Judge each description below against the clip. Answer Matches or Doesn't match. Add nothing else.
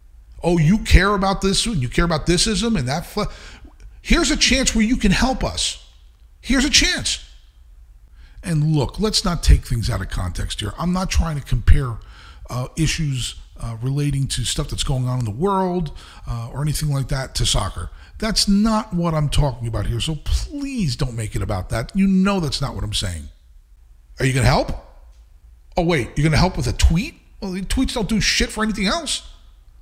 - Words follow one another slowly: Doesn't match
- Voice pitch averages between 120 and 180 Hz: Matches